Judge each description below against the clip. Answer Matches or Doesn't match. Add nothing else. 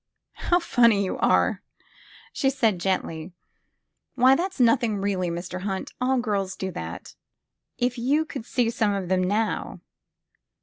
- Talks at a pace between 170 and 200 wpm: Doesn't match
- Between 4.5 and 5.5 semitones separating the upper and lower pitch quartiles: Matches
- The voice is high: Matches